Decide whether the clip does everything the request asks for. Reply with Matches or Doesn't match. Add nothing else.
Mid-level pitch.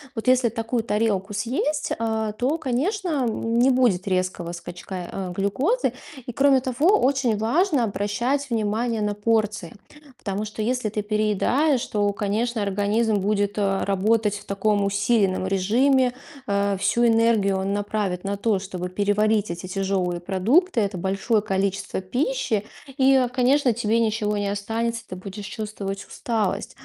Doesn't match